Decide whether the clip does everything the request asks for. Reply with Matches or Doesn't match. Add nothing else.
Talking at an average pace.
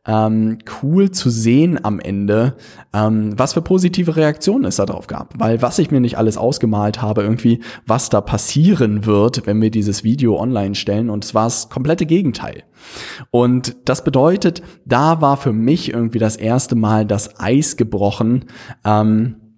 Matches